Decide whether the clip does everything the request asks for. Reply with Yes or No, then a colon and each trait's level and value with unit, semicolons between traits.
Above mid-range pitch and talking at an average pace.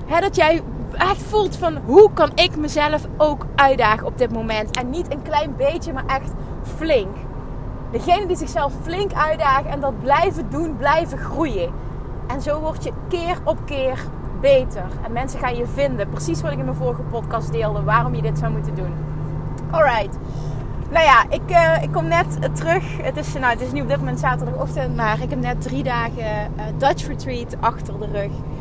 Yes: high, 215 Hz; average, 190 wpm